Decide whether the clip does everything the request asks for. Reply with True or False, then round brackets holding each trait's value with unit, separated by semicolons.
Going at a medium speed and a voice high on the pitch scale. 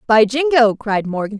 True (170 wpm; 230 Hz)